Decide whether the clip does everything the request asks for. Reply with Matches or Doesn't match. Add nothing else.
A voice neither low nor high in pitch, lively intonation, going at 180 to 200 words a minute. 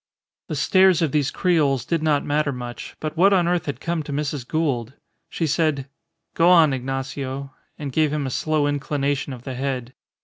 Doesn't match